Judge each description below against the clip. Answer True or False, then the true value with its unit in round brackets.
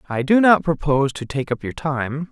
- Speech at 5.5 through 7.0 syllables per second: False (5.2 syllables/s)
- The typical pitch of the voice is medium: True (145 Hz)